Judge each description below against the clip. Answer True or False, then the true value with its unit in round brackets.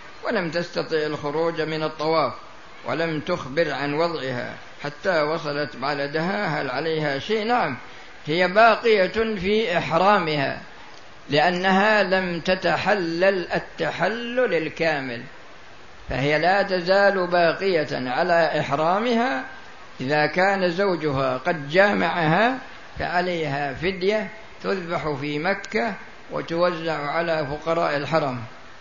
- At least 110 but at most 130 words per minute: False (95 wpm)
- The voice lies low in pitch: False (165 Hz)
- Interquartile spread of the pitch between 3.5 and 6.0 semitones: True (4.4 semitones)